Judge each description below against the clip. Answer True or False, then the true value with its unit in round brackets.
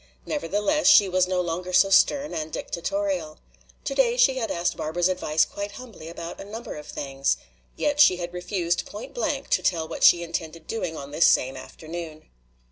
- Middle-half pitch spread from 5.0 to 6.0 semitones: True (5.3 semitones)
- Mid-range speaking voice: True (180 Hz)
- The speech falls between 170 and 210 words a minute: True (180 wpm)